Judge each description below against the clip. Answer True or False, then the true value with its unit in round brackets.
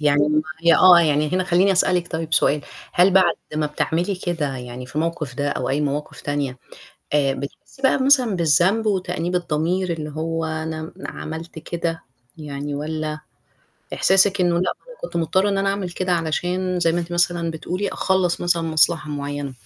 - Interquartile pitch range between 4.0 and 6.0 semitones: False (3.3 semitones)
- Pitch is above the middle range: False (165 Hz)